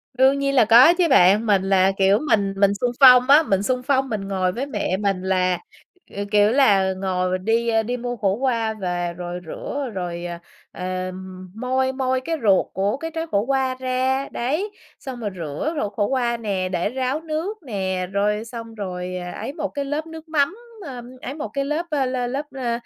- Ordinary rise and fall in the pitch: No, wide, 5.7 semitones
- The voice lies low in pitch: No, high, 230 Hz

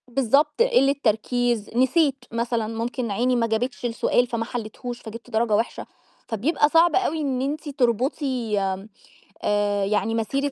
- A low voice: No, high, 245 Hz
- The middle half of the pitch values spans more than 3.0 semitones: Yes, average, 3.4 semitones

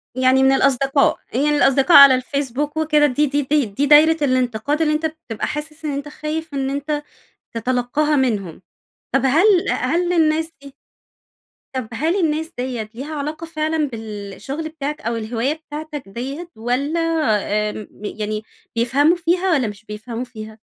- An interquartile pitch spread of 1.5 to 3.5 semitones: No, average, 4.0 semitones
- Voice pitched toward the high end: Yes, very high, 280 Hz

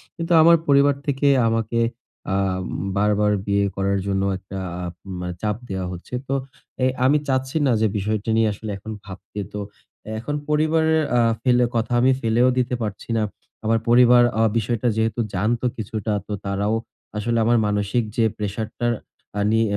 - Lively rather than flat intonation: No, average, 3.3 semitones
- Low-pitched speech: Yes, low, 115 Hz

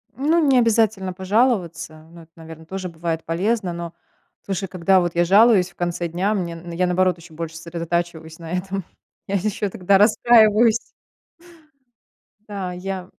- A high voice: No, medium, 180 Hz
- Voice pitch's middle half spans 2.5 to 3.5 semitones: Yes, average, 3.2 semitones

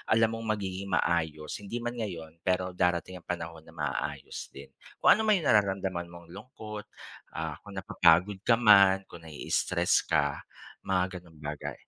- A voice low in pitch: Yes, very low, 90 Hz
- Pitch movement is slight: No, average, 4.0 semitones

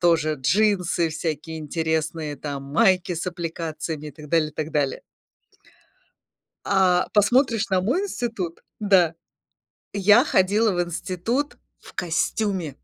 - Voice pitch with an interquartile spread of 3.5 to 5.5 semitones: Yes, average, 4.2 semitones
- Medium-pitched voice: Yes, medium, 175 Hz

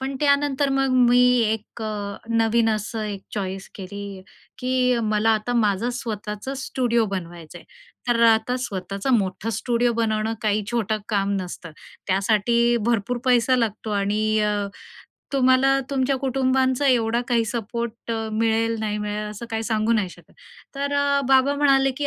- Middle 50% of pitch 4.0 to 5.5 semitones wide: No, average, 3.2 semitones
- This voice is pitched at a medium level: No, high, 230 Hz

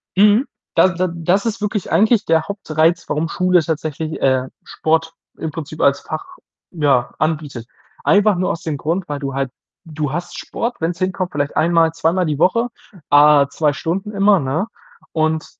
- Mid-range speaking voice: Yes, medium, 165 Hz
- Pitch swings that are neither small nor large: Yes, average, 3.7 semitones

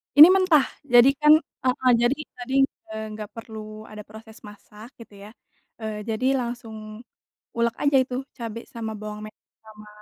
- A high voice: Yes, high, 230 Hz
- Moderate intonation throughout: Yes, average, 3.0 semitones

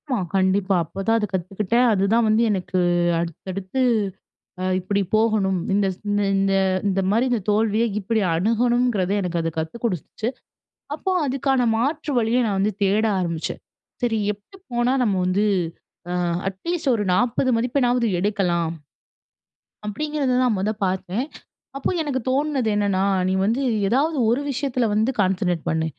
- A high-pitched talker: Yes, high, 210 Hz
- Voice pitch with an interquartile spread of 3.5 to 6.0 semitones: Yes, average, 4.4 semitones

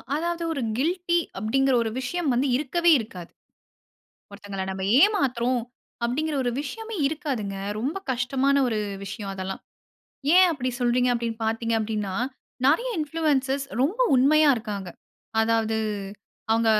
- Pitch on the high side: Yes, very high, 255 Hz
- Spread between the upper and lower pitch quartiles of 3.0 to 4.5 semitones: No, wide, 5.5 semitones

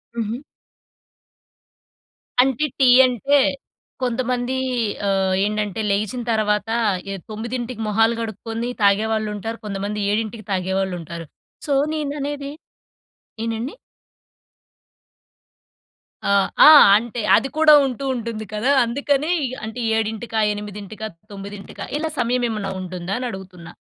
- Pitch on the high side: Yes, high, 220 Hz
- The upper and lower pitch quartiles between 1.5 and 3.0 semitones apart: No, average, 3.5 semitones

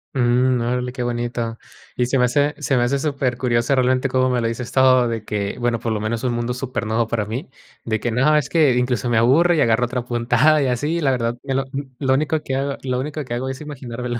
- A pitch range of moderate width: No, narrow, 2.2 semitones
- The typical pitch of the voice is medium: No, low, 125 Hz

